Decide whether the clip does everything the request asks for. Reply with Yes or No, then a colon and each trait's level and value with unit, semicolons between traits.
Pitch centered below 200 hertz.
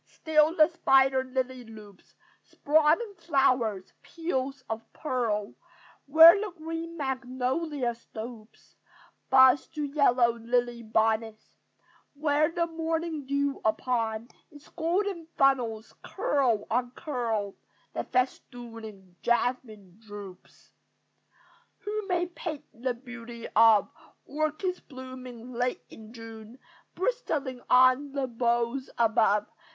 No: very high, 255 Hz